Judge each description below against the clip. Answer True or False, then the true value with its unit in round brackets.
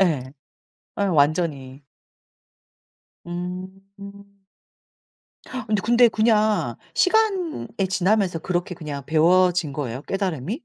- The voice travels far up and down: False (4.7 semitones)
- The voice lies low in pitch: False (185 Hz)